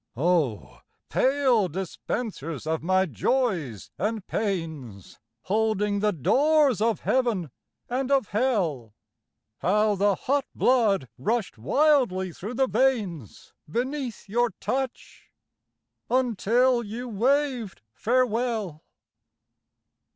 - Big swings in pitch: Yes, wide, 5.8 semitones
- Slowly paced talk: Yes, slow, 95 wpm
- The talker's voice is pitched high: Yes, high, 215 Hz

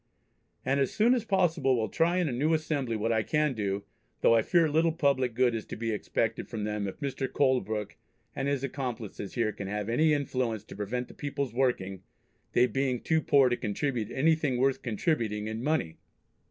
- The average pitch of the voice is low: Yes, low, 125 Hz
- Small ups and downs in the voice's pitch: No, average, 4.8 semitones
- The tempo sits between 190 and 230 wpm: Yes, average, 195 wpm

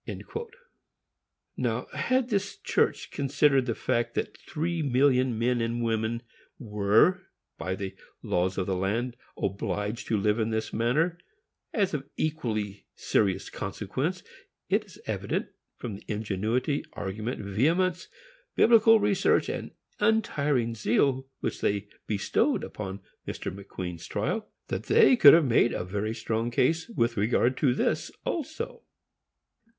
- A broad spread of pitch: Yes, wide, 6.6 semitones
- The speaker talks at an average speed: No, slow, 130 wpm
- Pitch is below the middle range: Yes, low, 120 Hz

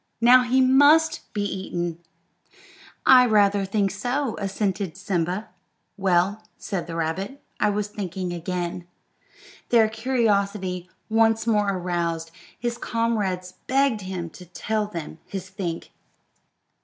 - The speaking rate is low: Yes, slow, 120 wpm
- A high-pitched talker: Yes, high, 200 Hz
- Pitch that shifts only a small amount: No, average, 3.8 semitones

